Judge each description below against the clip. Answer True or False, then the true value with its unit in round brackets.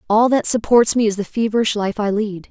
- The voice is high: True (215 Hz)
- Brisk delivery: True (240 wpm)